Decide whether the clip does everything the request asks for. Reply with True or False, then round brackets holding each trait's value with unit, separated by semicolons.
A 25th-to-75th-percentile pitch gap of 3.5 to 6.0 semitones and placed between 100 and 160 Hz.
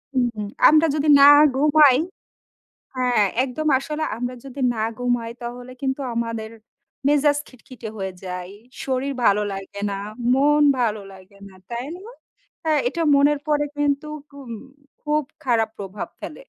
False (4.6 semitones; 255 Hz)